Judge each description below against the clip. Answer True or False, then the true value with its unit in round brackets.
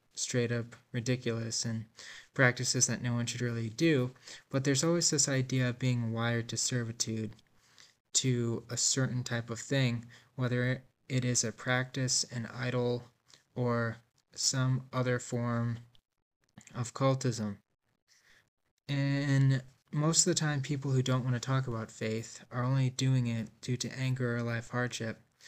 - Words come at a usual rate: True (150 wpm)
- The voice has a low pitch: True (125 Hz)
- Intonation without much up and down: True (1.9 semitones)